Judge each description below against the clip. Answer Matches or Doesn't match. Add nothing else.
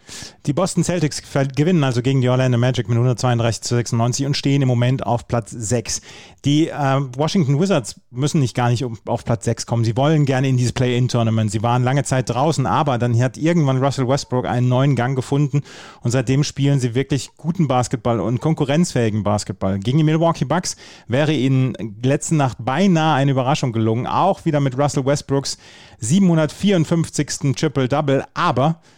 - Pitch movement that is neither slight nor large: Matches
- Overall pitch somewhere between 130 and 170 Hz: Matches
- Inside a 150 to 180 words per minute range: Matches